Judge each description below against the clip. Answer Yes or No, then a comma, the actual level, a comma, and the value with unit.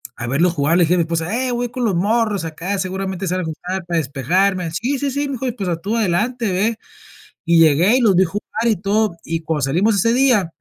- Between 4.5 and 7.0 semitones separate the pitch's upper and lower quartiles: Yes, average, 5.3 semitones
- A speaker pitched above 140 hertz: Yes, high, 190 Hz